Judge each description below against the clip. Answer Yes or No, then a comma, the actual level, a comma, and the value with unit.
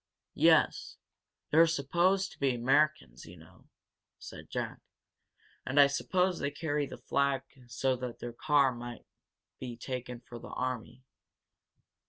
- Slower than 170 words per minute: Yes, slow, 135 wpm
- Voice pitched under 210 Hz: Yes, low, 135 Hz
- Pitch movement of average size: Yes, average, 3.5 semitones